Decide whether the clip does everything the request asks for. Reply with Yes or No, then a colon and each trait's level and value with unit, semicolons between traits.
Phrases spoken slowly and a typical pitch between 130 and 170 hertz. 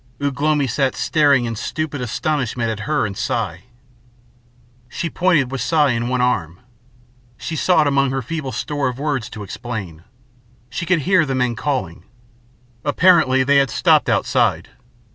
No: average, 155 wpm; low, 135 Hz